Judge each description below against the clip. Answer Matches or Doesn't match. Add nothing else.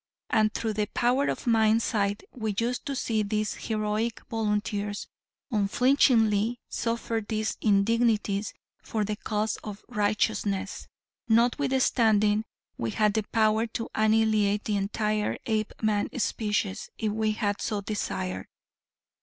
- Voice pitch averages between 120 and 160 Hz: Doesn't match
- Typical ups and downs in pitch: Doesn't match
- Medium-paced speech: Doesn't match